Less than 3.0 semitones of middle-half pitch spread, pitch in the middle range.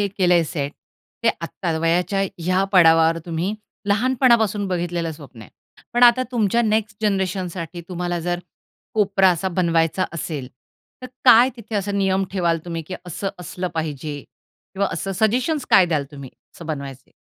No: average, 3.6 semitones; medium, 180 Hz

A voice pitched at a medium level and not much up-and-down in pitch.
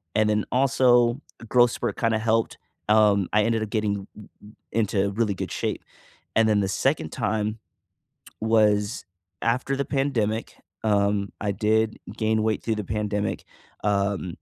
No: low, 110 Hz; narrow, 1.7 semitones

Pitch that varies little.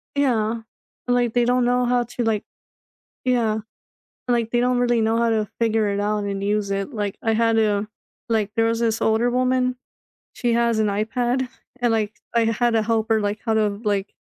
Yes: narrow, 2.2 semitones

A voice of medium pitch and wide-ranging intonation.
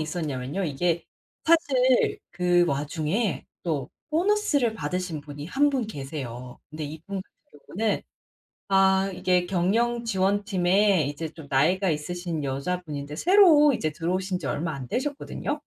Yes: medium, 180 Hz; wide, 6.1 semitones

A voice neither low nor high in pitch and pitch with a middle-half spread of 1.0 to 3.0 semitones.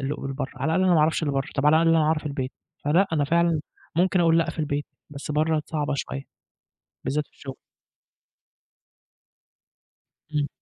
Yes: medium, 150 Hz; narrow, 2.4 semitones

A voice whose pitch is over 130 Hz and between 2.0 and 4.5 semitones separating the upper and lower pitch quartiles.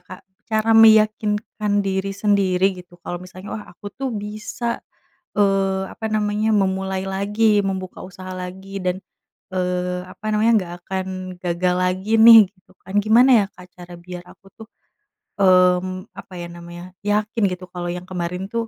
Yes: high, 190 Hz; narrow, 2.5 semitones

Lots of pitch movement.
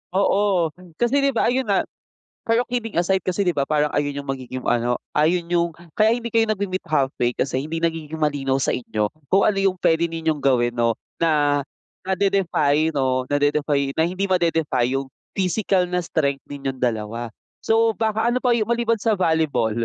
Yes: wide, 6.2 semitones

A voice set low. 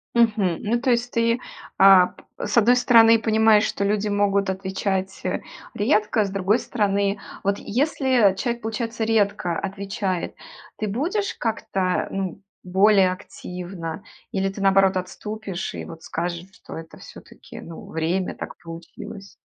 No: high, 200 Hz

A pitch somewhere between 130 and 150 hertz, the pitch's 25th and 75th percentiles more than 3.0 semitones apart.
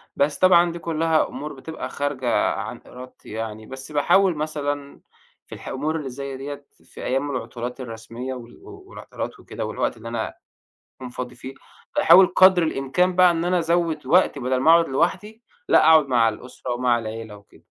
Yes: medium, 140 Hz; average, 4.9 semitones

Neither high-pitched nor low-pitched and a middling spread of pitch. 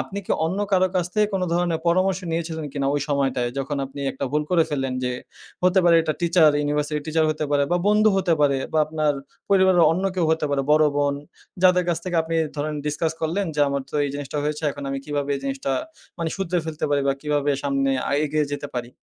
Yes: medium, 155 Hz; average, 3.4 semitones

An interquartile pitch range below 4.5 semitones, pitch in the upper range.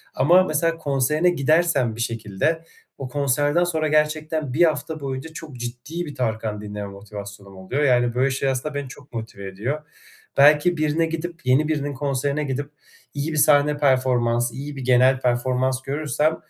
No: average, 3.7 semitones; medium, 140 Hz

